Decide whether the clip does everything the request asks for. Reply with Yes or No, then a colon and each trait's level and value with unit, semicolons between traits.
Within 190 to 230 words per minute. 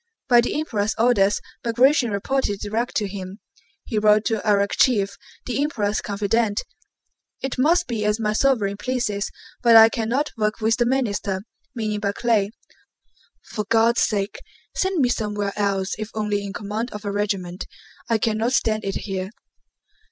No: average, 150 wpm